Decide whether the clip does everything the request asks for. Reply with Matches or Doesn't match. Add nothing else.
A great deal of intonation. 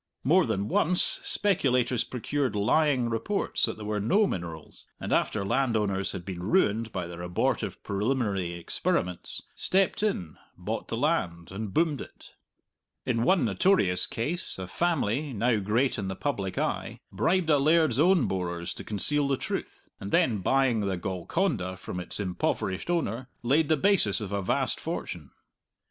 Matches